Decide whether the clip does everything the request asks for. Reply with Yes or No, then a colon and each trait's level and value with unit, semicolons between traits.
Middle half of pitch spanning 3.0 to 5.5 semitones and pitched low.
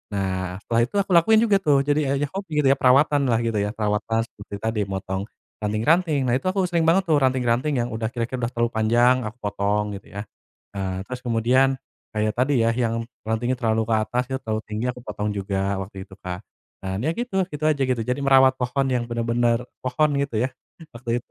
Yes: average, 4.1 semitones; low, 120 Hz